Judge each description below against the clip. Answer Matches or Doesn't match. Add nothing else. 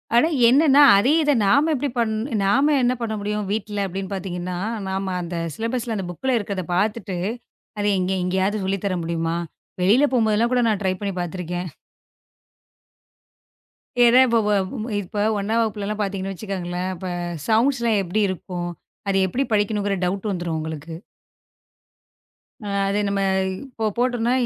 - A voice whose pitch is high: Matches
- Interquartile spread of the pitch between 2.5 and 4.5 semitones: Matches